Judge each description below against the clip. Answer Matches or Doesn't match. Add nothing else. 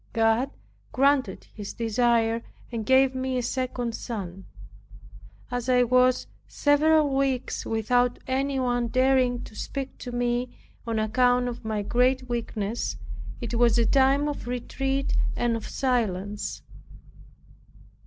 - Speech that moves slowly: Matches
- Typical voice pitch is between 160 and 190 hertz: Doesn't match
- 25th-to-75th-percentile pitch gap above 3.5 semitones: Doesn't match